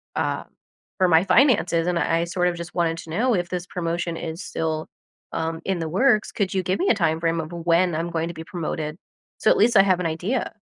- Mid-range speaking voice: Yes, medium, 170 Hz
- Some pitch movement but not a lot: No, narrow, 2.3 semitones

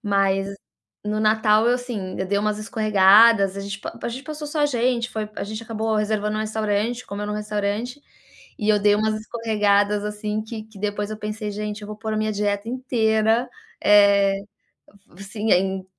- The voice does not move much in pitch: Yes, narrow, 1.4 semitones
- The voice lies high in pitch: Yes, high, 215 Hz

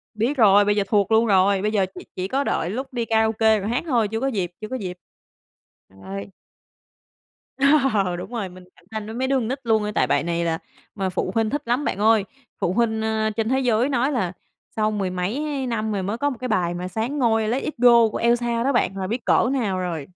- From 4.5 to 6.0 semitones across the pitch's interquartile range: No, average, 3.9 semitones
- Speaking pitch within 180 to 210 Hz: No, high, 220 Hz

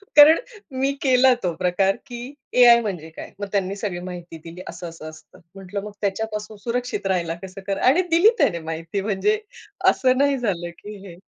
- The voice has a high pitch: Yes, high, 200 Hz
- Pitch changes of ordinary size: No, wide, 5.7 semitones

